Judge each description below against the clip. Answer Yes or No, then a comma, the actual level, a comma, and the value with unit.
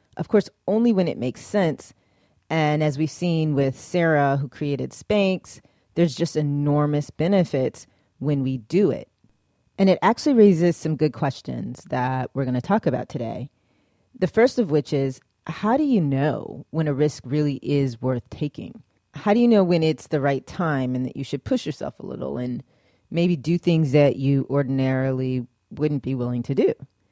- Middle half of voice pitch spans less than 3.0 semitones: No, average, 4.7 semitones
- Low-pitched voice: No, medium, 145 Hz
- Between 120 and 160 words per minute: No, average, 185 wpm